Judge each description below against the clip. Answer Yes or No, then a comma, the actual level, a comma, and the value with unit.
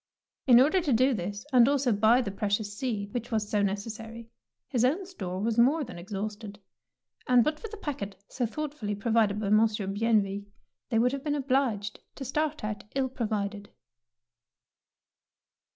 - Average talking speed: Yes, average, 165 wpm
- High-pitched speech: Yes, high, 225 Hz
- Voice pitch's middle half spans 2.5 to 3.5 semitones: No, average, 4.2 semitones